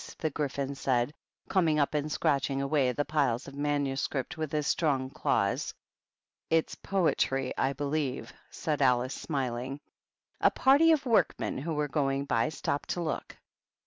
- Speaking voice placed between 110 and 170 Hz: Yes, medium, 140 Hz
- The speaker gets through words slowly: No, average, 160 wpm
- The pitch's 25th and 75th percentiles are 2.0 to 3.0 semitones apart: Yes, narrow, 2.5 semitones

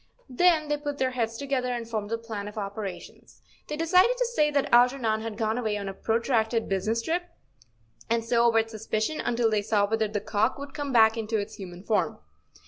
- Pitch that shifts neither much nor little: Yes, average, 4.0 semitones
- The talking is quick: Yes, fast, 210 wpm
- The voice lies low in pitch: No, high, 230 Hz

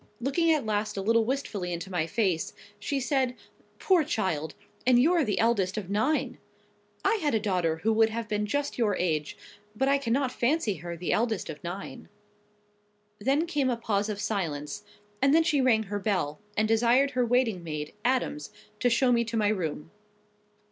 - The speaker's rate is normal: Yes, average, 180 wpm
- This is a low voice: No, high, 220 Hz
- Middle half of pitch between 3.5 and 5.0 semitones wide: No, wide, 5.4 semitones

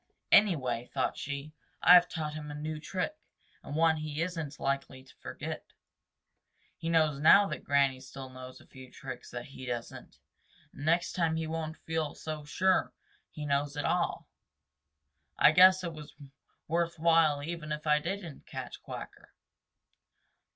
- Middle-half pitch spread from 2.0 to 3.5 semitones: Yes, average, 2.9 semitones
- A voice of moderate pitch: Yes, medium, 155 Hz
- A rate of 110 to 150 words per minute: No, average, 160 wpm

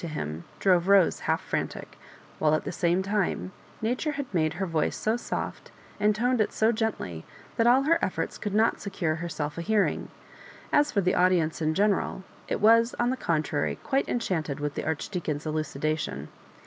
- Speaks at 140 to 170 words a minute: No, average, 185 wpm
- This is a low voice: No, medium, 185 Hz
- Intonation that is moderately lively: No, wide, 5.9 semitones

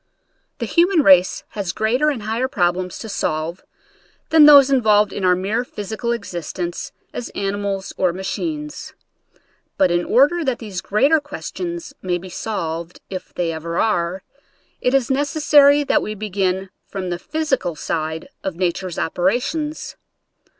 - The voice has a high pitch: Yes, high, 205 Hz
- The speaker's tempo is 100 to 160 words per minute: Yes, average, 150 wpm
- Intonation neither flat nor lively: No, wide, 7.3 semitones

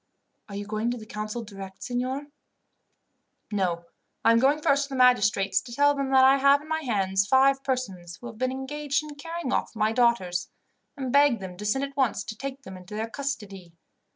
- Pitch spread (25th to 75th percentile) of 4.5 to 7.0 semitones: Yes, average, 5.1 semitones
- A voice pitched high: Yes, high, 245 Hz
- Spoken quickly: Yes, fast, 210 wpm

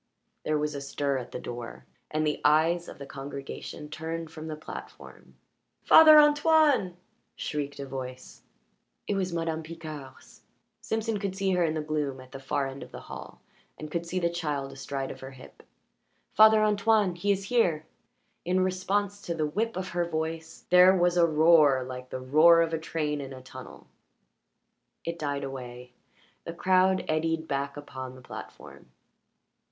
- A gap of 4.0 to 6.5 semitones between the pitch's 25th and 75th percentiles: Yes, average, 4.6 semitones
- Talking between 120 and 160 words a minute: No, average, 170 wpm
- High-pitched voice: No, medium, 160 Hz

